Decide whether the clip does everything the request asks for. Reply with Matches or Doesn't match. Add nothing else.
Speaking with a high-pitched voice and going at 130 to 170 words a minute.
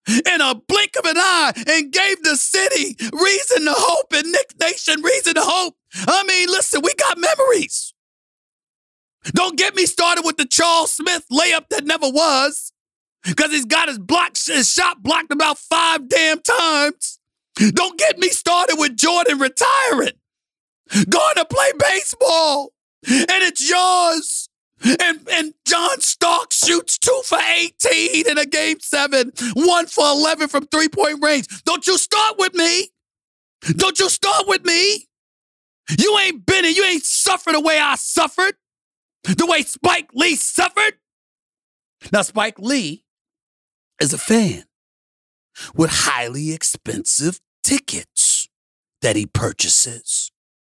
Matches